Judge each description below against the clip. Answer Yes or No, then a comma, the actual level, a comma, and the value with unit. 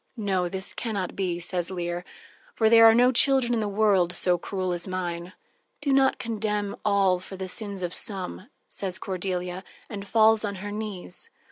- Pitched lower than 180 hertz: No, high, 195 Hz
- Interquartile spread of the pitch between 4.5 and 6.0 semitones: No, average, 3.2 semitones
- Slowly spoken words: No, average, 180 wpm